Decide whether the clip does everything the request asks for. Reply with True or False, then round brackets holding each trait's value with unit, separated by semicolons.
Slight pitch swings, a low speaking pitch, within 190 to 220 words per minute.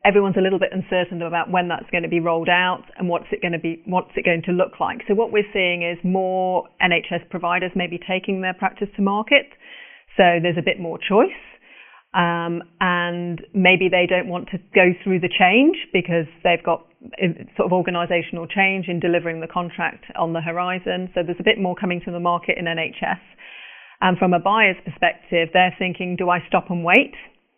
False (1.5 semitones; 180 Hz; 200 wpm)